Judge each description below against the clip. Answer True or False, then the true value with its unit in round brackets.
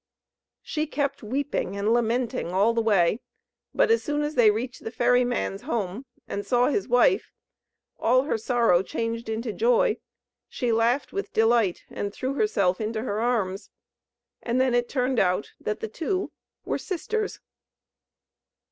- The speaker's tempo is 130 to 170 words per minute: True (155 wpm)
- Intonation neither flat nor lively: True (3.8 semitones)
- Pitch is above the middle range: True (240 Hz)